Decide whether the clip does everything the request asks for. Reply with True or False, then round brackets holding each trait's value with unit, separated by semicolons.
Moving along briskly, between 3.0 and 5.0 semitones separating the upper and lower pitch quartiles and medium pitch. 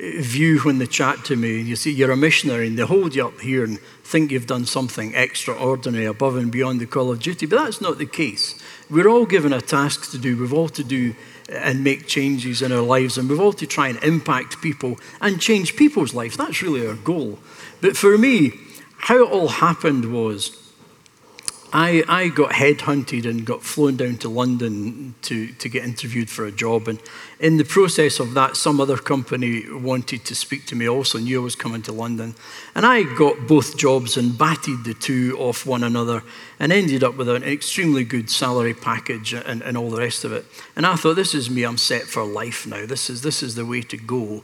False (220 wpm; 3.8 semitones; 130 Hz)